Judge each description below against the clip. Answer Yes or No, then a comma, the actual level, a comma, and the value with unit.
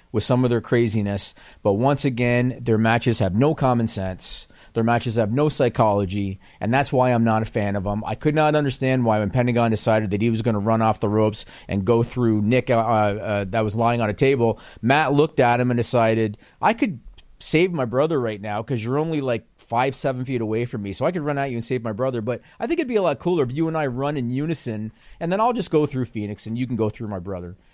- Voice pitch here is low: Yes, low, 120 Hz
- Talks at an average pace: No, fast, 255 wpm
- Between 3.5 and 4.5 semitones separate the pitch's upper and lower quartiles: Yes, average, 3.8 semitones